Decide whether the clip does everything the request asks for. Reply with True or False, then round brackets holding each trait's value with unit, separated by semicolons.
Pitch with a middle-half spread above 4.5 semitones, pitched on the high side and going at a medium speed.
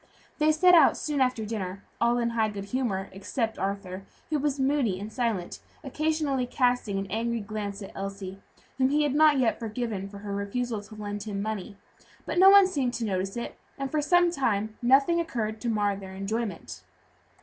True (5.2 semitones; 225 Hz; 190 wpm)